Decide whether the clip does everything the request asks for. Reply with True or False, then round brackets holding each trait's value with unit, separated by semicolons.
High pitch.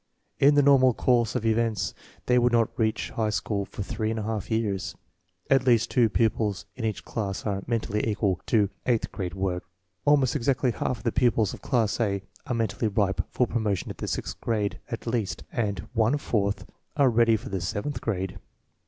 False (110 Hz)